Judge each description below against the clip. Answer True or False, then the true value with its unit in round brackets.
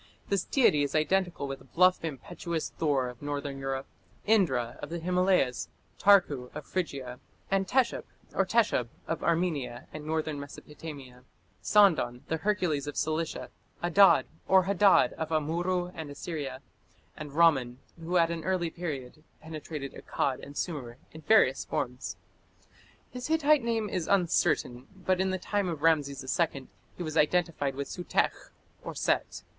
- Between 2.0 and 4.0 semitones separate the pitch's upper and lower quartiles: False (4.7 semitones)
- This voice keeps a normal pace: True (145 wpm)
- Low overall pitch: False (160 Hz)